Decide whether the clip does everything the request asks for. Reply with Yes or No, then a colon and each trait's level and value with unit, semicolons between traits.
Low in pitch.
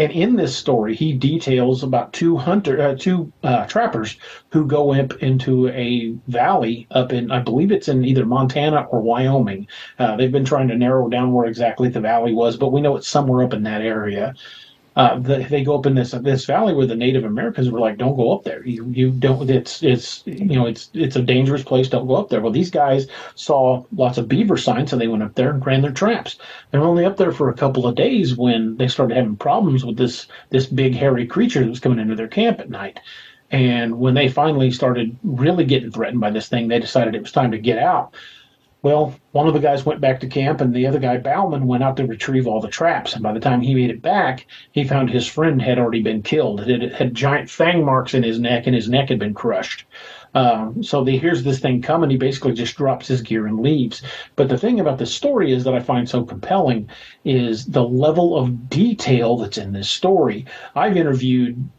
Yes: low, 130 Hz